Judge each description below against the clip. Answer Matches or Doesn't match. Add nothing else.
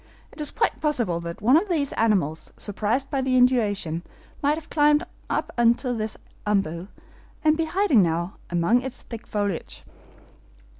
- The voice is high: Matches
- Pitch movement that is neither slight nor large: Doesn't match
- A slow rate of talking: Doesn't match